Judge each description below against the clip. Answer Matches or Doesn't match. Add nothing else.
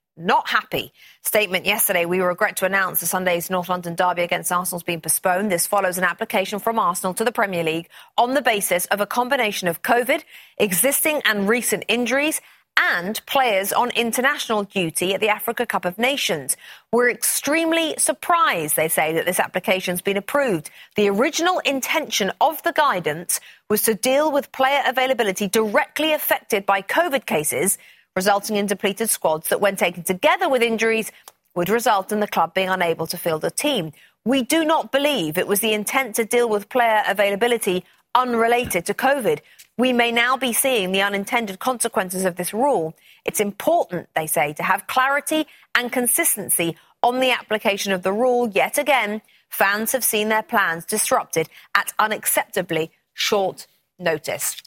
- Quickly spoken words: Doesn't match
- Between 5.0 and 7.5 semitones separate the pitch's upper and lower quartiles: Matches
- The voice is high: Matches